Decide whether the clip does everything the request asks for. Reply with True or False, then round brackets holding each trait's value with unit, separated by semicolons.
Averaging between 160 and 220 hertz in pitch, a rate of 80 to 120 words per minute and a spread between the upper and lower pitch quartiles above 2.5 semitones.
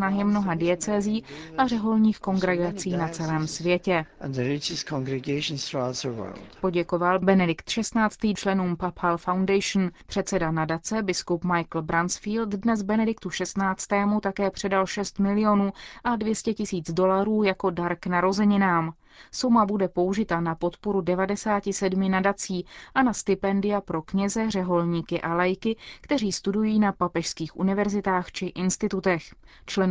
True (190 Hz; 115 wpm; 2.9 semitones)